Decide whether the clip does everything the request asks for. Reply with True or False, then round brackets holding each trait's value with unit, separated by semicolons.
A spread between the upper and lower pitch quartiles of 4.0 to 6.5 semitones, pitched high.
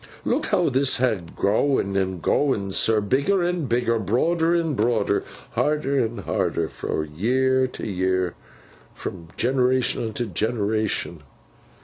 False (5.2 semitones; 120 Hz)